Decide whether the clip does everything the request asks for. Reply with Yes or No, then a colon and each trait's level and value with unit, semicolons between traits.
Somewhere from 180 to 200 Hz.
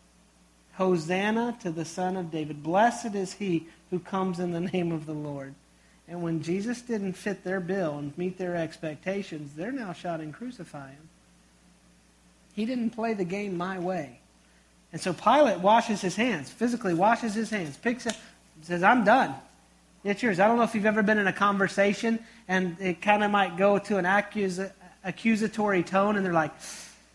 Yes: medium, 185 Hz